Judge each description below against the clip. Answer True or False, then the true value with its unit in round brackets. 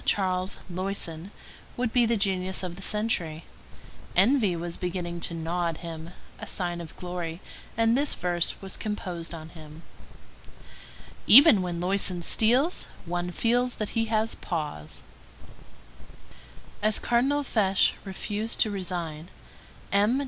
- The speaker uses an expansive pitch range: False (4.1 semitones)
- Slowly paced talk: True (125 wpm)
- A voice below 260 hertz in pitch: True (185 Hz)